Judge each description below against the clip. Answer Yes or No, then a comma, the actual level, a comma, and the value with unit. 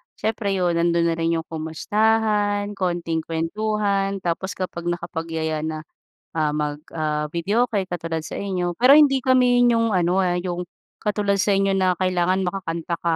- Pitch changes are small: No, average, 3.6 semitones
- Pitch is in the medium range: Yes, medium, 180 Hz